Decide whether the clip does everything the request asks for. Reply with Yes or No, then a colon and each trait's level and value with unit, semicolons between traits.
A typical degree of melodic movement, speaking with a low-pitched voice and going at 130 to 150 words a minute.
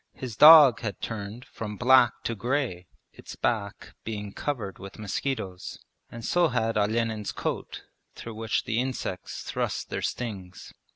Yes: average, 3.3 semitones; low, 115 Hz; average, 140 wpm